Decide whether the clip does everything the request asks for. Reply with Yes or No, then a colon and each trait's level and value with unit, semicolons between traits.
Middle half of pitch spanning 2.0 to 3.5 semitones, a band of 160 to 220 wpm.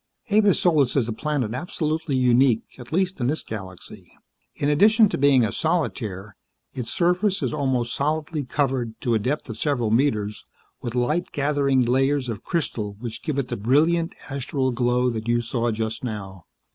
No: average, 4.6 semitones; average, 170 wpm